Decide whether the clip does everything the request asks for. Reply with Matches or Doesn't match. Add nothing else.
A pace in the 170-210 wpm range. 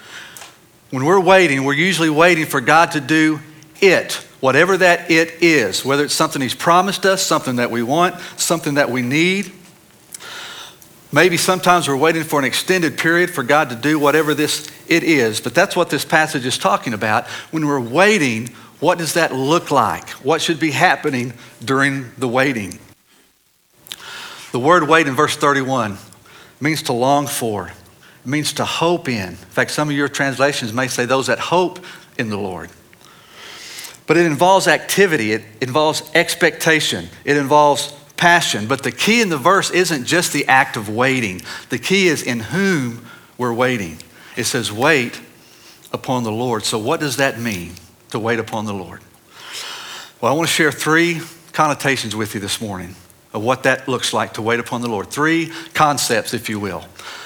Matches